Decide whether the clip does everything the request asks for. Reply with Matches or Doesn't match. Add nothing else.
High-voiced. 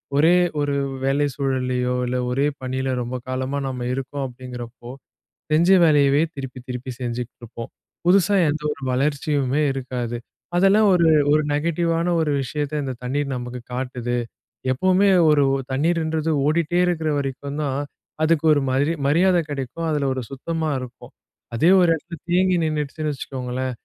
Doesn't match